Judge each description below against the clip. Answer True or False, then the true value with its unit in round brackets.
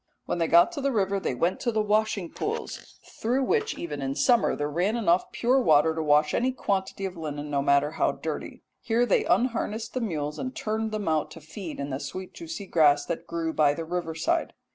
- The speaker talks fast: True (220 wpm)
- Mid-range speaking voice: True (175 Hz)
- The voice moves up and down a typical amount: False (6.6 semitones)